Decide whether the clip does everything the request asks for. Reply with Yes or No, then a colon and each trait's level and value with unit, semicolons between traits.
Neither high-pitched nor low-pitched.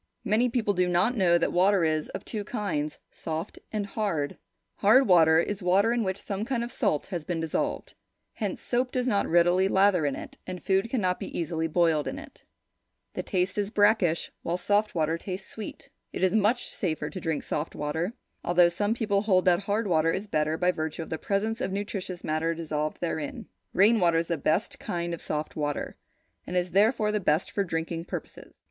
Yes: medium, 180 Hz